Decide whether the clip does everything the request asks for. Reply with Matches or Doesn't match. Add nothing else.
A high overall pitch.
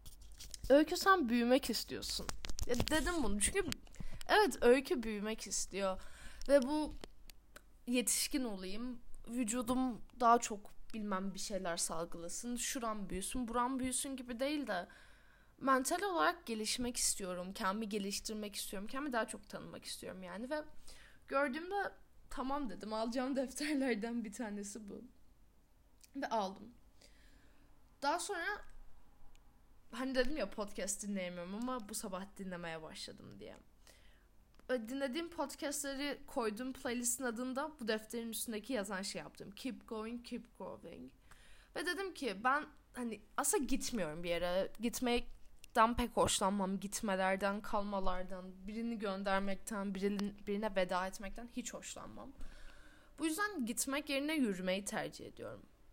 Matches